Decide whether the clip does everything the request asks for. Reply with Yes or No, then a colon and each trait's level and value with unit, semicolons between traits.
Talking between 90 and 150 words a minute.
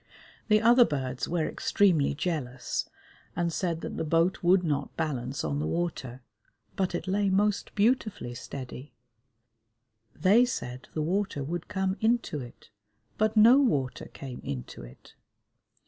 Yes: average, 140 wpm